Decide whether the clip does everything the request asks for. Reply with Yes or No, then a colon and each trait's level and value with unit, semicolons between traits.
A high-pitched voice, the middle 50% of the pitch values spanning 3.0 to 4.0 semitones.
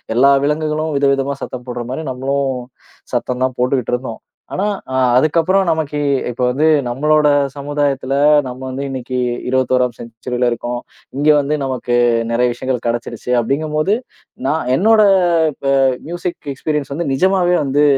No: low, 135 Hz; average, 3.3 semitones